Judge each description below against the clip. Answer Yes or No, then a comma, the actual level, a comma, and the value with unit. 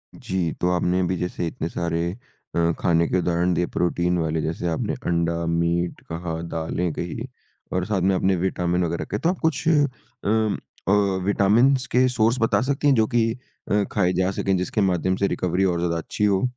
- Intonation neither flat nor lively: Yes, average, 3.5 semitones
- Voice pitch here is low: Yes, very low, 90 Hz